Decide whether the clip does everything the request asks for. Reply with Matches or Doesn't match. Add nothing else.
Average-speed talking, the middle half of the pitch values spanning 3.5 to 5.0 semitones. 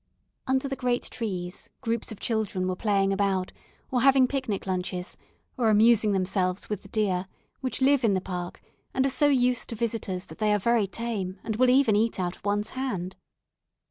Matches